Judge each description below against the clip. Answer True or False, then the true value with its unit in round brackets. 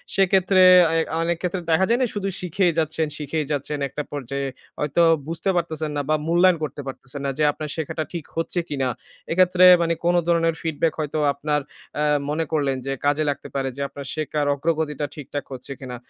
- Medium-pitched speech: True (155 Hz)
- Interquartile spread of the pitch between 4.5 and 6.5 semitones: False (2.9 semitones)